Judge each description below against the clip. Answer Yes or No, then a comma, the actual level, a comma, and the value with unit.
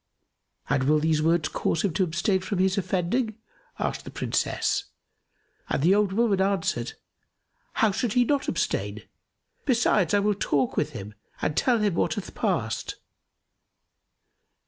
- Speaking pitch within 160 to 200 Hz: Yes, high, 190 Hz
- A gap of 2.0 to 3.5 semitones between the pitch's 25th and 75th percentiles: No, average, 4.6 semitones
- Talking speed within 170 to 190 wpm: No, average, 145 wpm